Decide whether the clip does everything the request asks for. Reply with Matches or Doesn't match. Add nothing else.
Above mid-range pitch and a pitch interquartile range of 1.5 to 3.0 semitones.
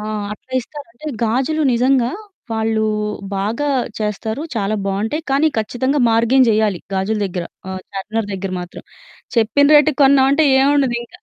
Doesn't match